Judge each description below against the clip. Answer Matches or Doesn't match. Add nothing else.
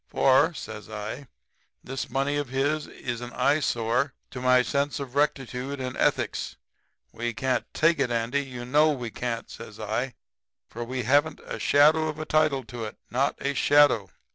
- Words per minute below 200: Matches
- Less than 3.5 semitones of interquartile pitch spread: Matches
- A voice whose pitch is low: Matches